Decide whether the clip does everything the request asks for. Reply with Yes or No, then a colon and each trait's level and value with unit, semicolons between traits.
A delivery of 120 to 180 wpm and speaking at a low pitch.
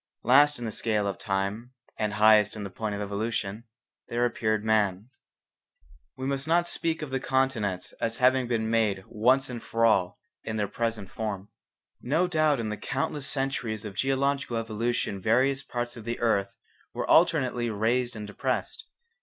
Yes: average, 165 wpm; low, 115 Hz